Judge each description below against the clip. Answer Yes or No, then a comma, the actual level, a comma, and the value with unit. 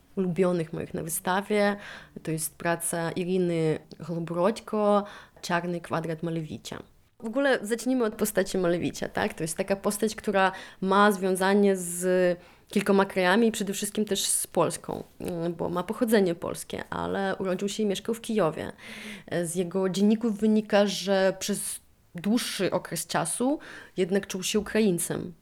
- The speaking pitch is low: No, high, 190 Hz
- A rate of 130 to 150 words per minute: Yes, average, 140 wpm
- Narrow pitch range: No, average, 3.1 semitones